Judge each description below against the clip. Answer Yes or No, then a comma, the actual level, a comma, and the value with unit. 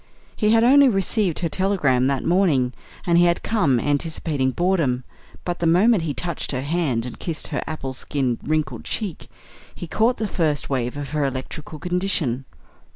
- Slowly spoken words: No, average, 170 wpm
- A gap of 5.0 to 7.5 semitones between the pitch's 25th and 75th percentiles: Yes, wide, 5.4 semitones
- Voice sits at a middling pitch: Yes, medium, 160 Hz